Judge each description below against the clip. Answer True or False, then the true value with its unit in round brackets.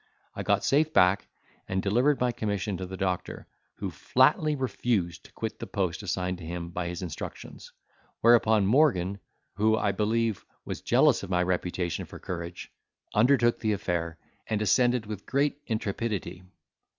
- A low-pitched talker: True (100 Hz)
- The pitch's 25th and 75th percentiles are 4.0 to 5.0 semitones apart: True (4.4 semitones)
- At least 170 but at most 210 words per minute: False (155 wpm)